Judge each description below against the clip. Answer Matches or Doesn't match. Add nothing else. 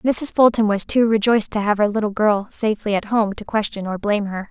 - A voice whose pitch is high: Matches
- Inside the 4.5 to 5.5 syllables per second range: Doesn't match